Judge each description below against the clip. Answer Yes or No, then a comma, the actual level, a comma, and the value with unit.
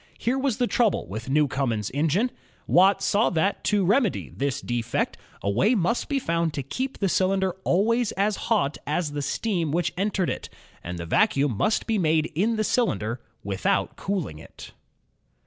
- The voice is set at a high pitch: No, medium, 175 Hz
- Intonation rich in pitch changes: Yes, wide, 7.2 semitones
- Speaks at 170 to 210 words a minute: Yes, average, 175 wpm